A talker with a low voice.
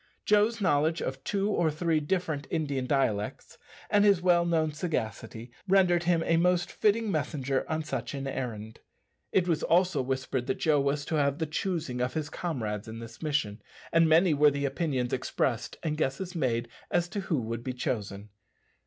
No: medium, 150 Hz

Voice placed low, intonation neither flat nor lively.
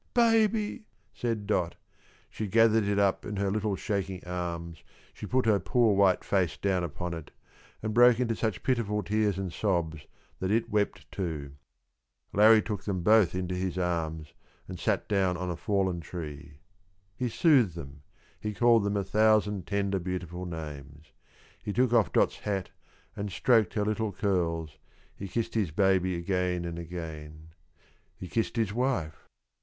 Yes: very low, 95 Hz; average, 3.8 semitones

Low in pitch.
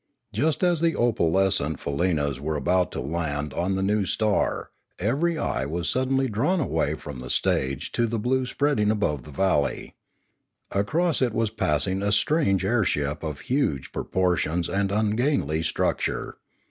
Yes: very low, 95 Hz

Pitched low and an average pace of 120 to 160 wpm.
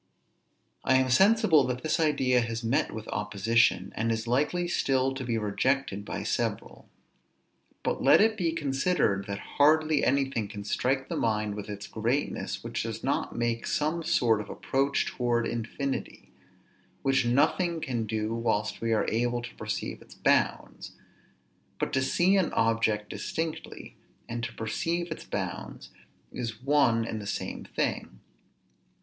Yes: low, 120 Hz; average, 150 wpm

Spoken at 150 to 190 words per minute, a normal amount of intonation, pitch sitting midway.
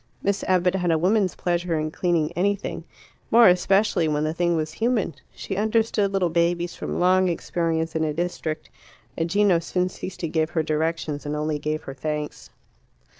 Yes: average, 175 wpm; average, 3.0 semitones; medium, 170 Hz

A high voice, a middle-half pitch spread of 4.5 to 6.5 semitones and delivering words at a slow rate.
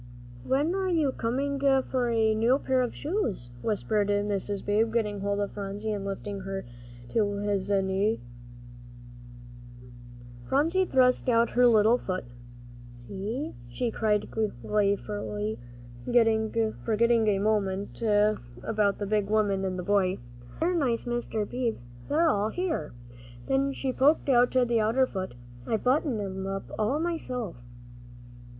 No: high, 220 Hz; average, 3.9 semitones; slow, 130 wpm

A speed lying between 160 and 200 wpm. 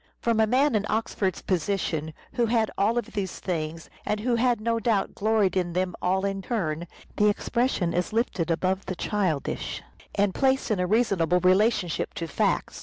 Yes: average, 180 wpm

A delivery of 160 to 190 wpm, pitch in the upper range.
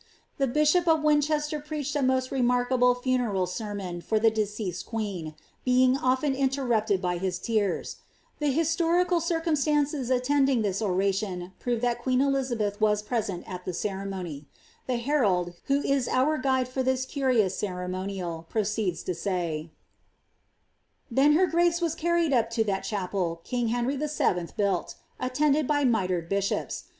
No: average, 150 wpm; high, 240 Hz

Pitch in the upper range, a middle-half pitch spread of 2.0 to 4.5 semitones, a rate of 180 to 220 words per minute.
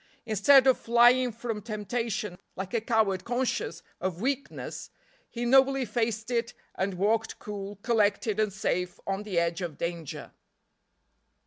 No: high, 215 Hz; average, 3.7 semitones; slow, 135 wpm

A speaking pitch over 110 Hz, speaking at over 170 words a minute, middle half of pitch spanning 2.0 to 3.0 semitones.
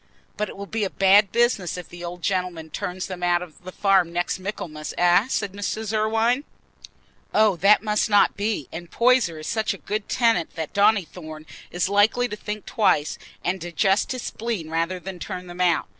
No: high, 190 Hz; average, 190 wpm; average, 3.4 semitones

